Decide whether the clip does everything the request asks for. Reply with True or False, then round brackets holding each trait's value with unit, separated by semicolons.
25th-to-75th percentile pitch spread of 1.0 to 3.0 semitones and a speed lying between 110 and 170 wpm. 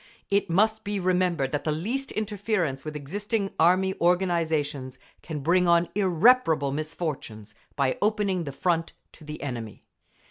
False (4.9 semitones; 140 wpm)